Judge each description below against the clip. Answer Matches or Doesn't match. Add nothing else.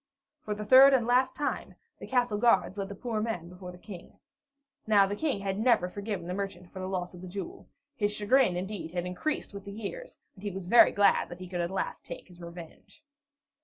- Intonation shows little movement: Doesn't match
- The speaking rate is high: Matches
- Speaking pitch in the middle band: Doesn't match